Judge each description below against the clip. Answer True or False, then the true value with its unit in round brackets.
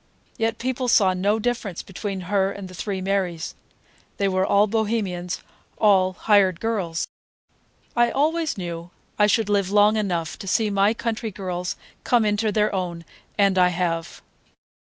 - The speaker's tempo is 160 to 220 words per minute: False (150 wpm)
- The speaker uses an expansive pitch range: False (3.0 semitones)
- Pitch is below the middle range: False (200 Hz)